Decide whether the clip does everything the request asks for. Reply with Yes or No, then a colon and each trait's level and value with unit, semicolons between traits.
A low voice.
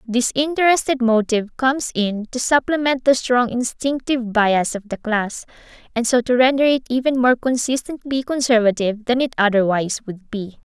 No: high, 240 Hz